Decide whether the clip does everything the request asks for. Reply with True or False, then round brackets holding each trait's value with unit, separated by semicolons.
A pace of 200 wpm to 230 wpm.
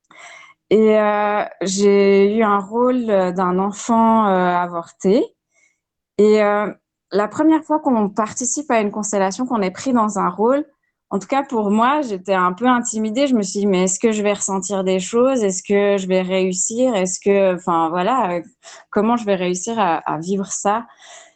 False (180 wpm)